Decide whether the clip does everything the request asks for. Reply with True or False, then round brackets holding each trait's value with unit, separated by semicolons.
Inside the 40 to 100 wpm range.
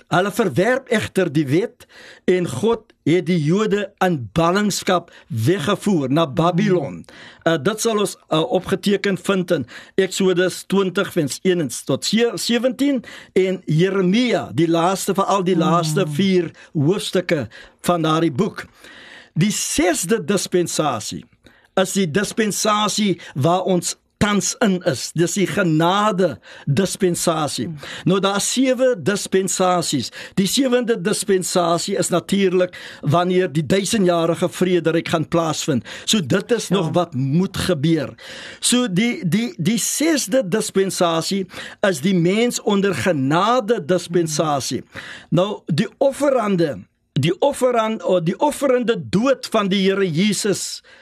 False (120 wpm)